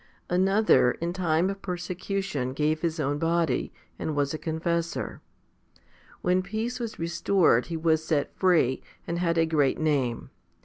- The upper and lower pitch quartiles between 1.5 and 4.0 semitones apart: Yes, average, 2.9 semitones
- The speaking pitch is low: No, medium, 165 Hz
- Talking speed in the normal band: Yes, average, 150 wpm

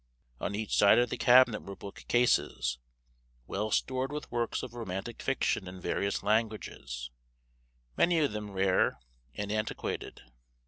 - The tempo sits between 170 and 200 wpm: No, average, 140 wpm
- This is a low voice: Yes, low, 110 Hz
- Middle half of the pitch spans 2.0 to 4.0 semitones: Yes, average, 3.7 semitones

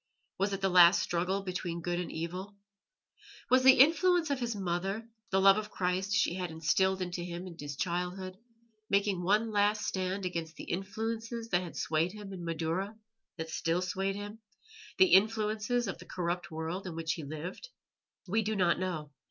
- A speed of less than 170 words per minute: No, average, 180 wpm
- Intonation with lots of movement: No, average, 3.2 semitones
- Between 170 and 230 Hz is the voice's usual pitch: Yes, medium, 185 Hz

